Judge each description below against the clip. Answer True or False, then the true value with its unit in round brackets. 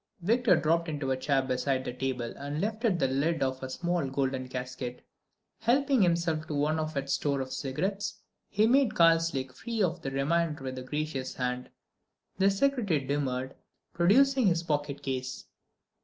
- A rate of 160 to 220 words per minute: True (165 wpm)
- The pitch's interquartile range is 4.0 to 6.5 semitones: True (5.1 semitones)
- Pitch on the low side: False (150 Hz)